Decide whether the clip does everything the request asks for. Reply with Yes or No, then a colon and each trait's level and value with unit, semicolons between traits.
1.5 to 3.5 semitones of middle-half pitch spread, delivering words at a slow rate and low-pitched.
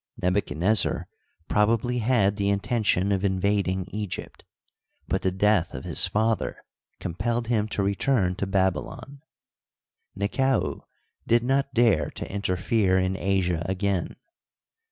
Yes: average, 3.2 semitones; slow, 120 wpm; low, 100 Hz